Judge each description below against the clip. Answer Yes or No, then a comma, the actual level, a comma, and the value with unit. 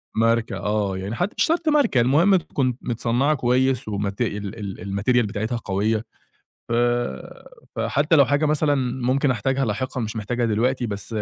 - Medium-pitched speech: No, low, 120 Hz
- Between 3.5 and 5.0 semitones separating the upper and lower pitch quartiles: Yes, average, 4.3 semitones